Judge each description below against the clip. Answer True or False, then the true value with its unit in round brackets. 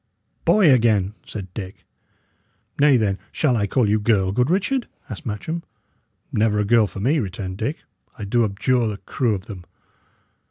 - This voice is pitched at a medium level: False (110 Hz)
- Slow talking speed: False (165 wpm)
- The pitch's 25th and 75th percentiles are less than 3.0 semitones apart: False (4.4 semitones)